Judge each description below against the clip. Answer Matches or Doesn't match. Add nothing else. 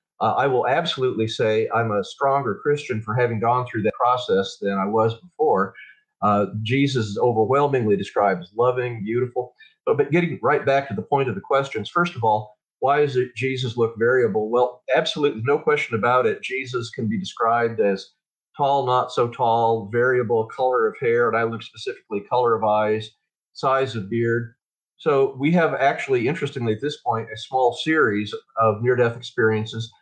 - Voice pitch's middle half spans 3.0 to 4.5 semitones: Matches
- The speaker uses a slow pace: Doesn't match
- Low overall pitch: Matches